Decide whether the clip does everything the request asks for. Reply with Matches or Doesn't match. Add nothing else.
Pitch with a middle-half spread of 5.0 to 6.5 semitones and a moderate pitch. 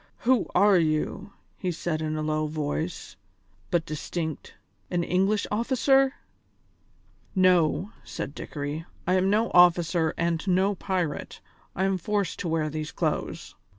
Doesn't match